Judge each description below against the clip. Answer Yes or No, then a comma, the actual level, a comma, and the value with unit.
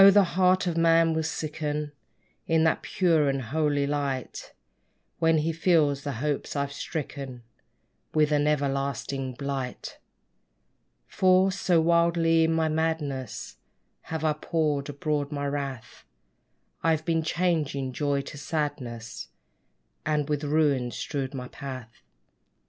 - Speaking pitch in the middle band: Yes, medium, 150 Hz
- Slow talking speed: Yes, slow, 125 wpm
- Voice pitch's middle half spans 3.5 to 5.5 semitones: No, average, 2.7 semitones